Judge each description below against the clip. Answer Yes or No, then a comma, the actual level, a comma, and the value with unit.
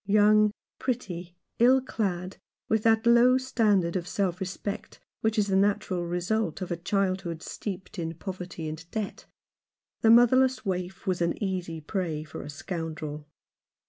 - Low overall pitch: No, high, 190 Hz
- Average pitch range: Yes, average, 4.0 semitones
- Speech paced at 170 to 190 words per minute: No, average, 145 wpm